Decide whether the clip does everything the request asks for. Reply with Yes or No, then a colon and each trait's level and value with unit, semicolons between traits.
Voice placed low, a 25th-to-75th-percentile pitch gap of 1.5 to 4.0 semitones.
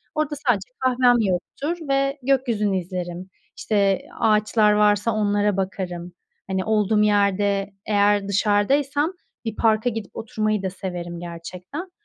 No: high, 205 Hz; average, 3.2 semitones